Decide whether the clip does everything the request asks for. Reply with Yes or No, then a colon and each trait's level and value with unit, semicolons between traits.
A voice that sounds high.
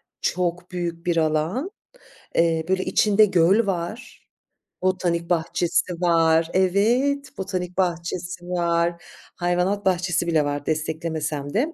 No: medium, 175 Hz